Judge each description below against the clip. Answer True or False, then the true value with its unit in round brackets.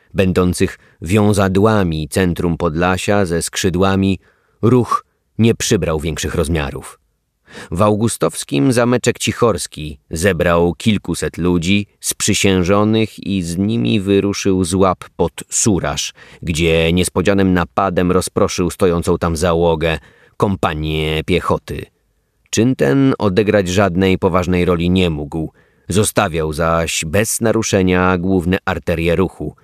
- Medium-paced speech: False (105 wpm)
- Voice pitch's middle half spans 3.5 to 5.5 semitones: False (3.0 semitones)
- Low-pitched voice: True (95 Hz)